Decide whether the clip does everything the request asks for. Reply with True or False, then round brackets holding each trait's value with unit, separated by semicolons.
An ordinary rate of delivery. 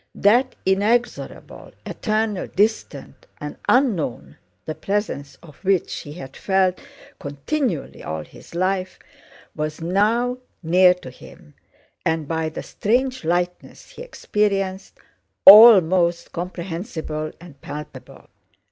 False (105 wpm)